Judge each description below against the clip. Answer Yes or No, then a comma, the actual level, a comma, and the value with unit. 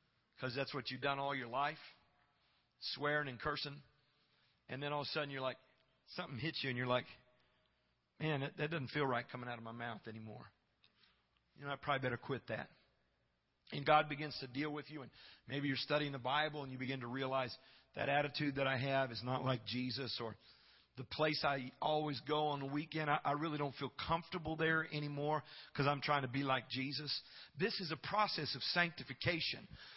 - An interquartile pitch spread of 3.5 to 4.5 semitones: No, narrow, 2.6 semitones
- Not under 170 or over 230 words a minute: Yes, average, 200 wpm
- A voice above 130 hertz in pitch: Yes, medium, 140 Hz